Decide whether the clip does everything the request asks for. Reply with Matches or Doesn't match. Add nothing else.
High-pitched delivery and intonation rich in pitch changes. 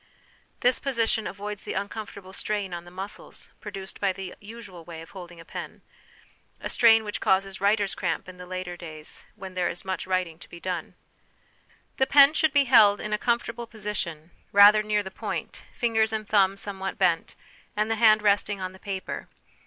Doesn't match